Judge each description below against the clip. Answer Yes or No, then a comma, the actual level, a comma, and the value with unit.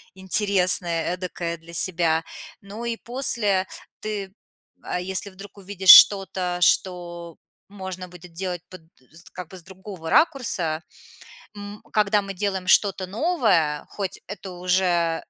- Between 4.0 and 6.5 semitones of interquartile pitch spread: No, narrow, 2.5 semitones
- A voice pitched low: No, medium, 185 Hz